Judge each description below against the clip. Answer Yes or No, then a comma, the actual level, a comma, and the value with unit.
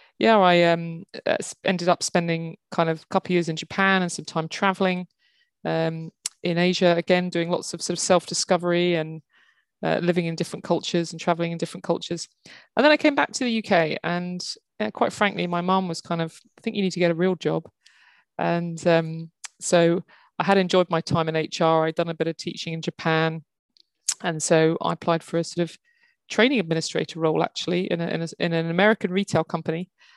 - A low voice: No, medium, 175 Hz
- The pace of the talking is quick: Yes, fast, 210 wpm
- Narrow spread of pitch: Yes, narrow, 2.2 semitones